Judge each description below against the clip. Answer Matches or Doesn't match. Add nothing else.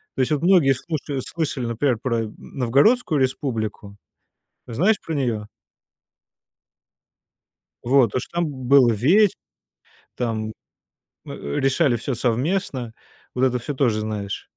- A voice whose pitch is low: Matches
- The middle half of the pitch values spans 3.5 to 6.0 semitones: Matches